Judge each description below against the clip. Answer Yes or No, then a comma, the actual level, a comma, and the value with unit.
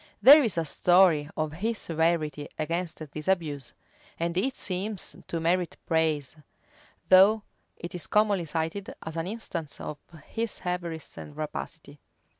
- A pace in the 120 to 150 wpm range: Yes, average, 140 wpm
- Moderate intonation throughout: Yes, average, 3.4 semitones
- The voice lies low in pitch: No, medium, 170 Hz